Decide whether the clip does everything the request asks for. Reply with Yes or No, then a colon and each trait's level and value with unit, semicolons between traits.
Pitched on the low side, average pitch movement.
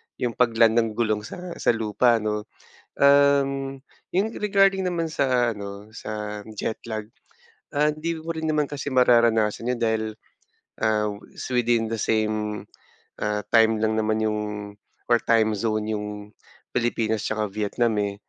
Yes: low, 115 Hz; average, 3.7 semitones